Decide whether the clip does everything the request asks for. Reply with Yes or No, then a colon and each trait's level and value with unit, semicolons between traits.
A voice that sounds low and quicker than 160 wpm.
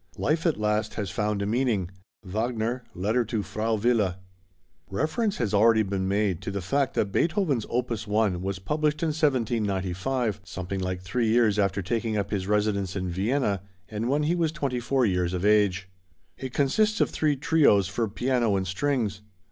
Yes: low, 110 Hz; average, 175 wpm